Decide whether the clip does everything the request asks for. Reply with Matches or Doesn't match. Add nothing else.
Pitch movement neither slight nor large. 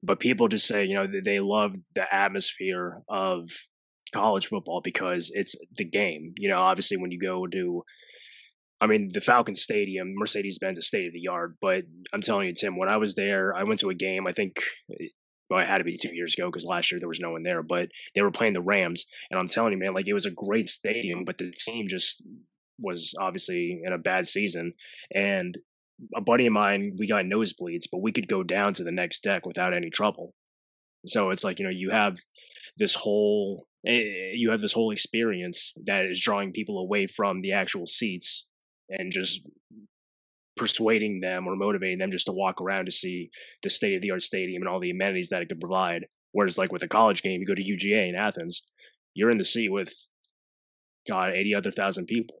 Matches